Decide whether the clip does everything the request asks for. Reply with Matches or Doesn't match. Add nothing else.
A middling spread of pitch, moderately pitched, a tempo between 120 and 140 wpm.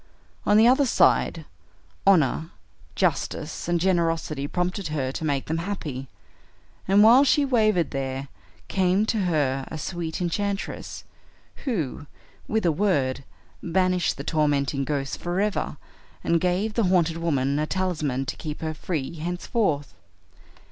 Matches